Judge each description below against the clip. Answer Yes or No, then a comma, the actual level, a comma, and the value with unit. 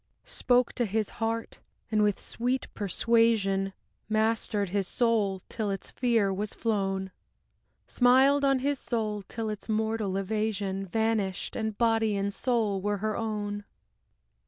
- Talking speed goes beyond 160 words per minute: No, slow, 135 wpm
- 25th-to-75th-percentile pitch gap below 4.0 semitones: Yes, narrow, 2.4 semitones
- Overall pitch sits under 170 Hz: No, high, 215 Hz